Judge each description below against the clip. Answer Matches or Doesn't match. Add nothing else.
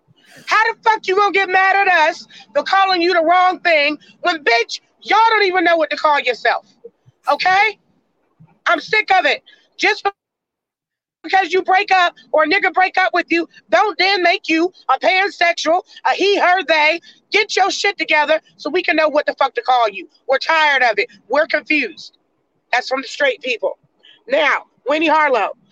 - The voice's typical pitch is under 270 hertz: Doesn't match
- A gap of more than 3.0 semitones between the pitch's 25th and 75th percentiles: Matches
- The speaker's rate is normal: Matches